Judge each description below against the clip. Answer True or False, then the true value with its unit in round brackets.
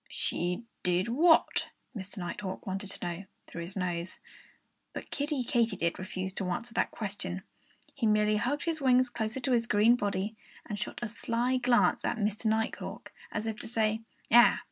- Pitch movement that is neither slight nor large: True (4.0 semitones)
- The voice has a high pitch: True (215 Hz)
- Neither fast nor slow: True (170 wpm)